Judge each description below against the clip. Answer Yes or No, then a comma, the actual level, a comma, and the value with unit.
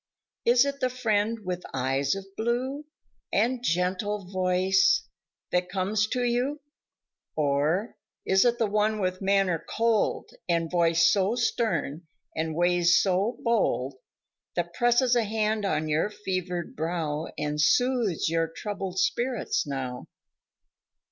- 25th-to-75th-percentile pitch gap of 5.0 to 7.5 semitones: Yes, wide, 5.4 semitones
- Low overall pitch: No, high, 195 Hz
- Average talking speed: No, slow, 130 wpm